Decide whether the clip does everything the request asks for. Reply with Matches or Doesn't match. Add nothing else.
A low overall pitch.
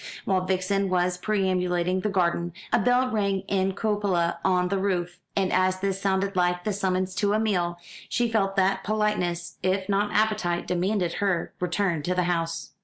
Doesn't match